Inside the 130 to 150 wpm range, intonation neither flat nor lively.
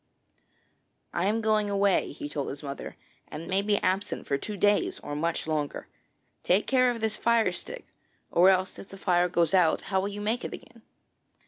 No: average, 190 wpm; average, 3.8 semitones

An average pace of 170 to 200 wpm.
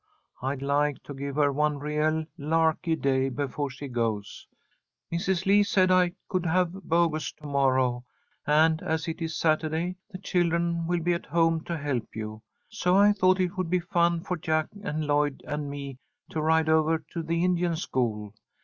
Yes: average, 180 wpm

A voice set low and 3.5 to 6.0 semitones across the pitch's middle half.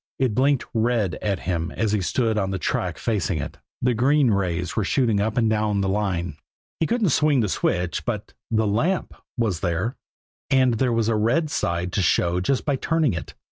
Yes: low, 110 Hz; average, 5.1 semitones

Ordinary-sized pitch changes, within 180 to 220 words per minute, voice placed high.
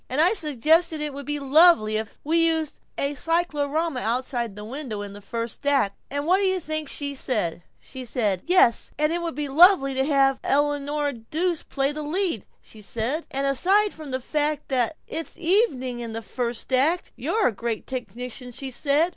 Yes: average, 4.4 semitones; average, 185 wpm; very high, 280 Hz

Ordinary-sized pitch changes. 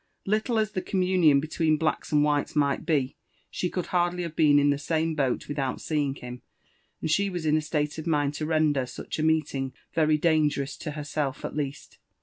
No: narrow, 2.2 semitones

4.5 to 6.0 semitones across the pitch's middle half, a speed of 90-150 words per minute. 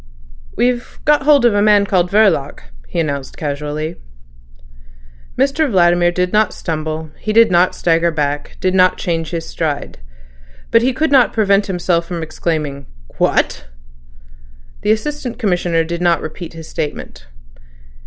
Yes: average, 5.1 semitones; average, 140 wpm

